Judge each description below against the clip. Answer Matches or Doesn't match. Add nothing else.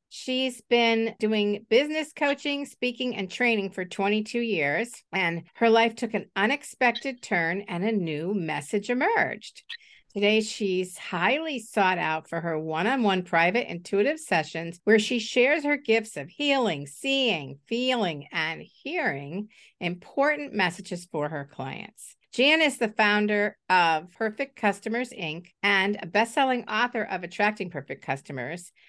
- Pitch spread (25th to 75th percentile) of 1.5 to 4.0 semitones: Doesn't match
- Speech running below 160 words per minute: Matches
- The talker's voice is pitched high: Matches